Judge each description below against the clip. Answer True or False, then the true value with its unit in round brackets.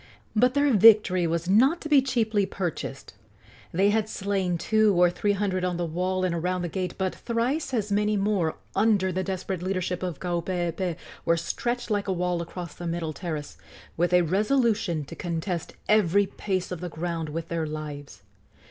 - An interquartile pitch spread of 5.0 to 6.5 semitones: False (3.4 semitones)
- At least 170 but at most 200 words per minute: True (180 wpm)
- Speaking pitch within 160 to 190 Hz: True (185 Hz)